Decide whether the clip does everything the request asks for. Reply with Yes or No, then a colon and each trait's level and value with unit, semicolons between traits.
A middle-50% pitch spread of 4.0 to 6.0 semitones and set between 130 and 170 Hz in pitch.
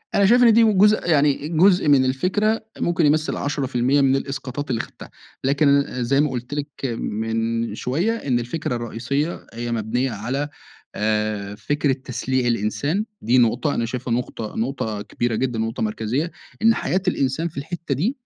Yes: average, 4.8 semitones; low, 135 Hz